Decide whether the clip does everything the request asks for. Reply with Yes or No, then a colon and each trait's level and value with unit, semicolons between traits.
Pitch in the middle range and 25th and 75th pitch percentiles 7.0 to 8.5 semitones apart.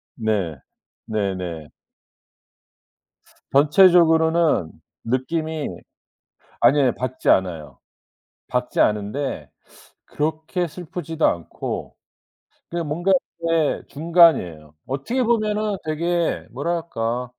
Yes: medium, 150 Hz; wide, 7.4 semitones